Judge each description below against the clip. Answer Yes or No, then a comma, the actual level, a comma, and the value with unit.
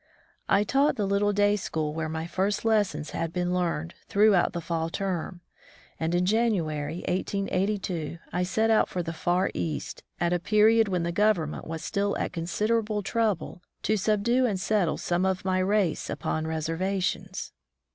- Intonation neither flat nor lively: Yes, average, 3.7 semitones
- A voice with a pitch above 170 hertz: Yes, medium, 185 Hz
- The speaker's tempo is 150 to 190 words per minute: Yes, average, 165 wpm